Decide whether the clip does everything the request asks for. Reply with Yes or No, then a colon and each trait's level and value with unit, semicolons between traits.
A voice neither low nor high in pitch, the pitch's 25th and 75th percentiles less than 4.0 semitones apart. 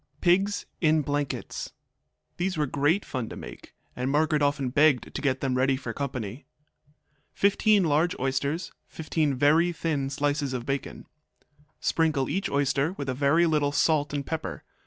Yes: medium, 145 Hz; average, 2.9 semitones